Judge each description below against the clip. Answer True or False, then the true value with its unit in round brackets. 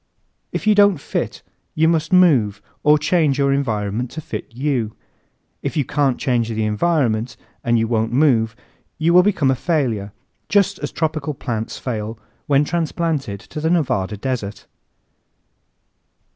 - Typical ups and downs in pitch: False (5.9 semitones)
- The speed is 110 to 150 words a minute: True (145 wpm)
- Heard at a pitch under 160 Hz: True (135 Hz)